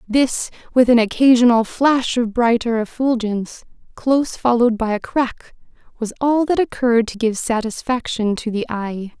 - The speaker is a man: No, female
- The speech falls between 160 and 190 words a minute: No, average, 150 wpm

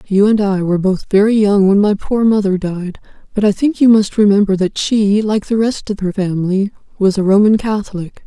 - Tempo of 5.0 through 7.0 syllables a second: Yes, 5.3 syllables/s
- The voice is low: No, high, 205 Hz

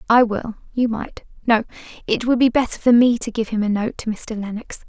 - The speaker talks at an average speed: No, fast, 210 wpm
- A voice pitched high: Yes, high, 230 Hz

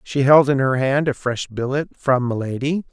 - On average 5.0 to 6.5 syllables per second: No, 4.7 syllables/s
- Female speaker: No, male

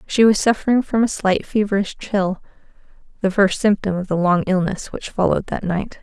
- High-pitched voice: Yes, high, 200 Hz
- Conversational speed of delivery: Yes, average, 180 wpm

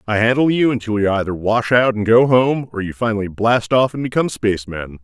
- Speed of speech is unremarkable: No, fast, 225 wpm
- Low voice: Yes, low, 115 Hz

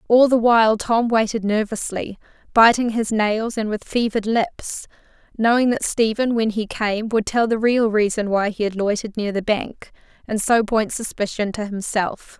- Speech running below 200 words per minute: Yes, average, 180 wpm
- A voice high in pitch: Yes, high, 220 Hz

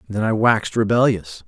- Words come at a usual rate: Yes, average, 160 wpm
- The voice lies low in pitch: Yes, low, 105 Hz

